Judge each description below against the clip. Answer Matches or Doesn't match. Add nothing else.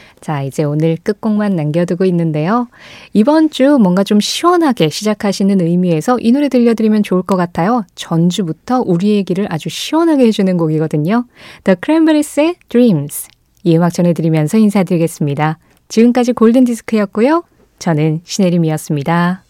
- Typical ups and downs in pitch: Doesn't match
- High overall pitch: Matches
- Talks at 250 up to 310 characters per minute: Doesn't match